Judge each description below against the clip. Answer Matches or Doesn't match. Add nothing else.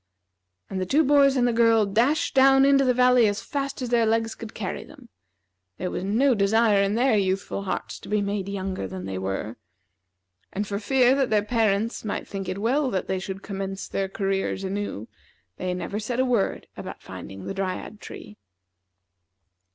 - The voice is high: Matches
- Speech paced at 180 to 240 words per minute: Matches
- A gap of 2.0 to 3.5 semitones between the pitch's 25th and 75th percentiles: Doesn't match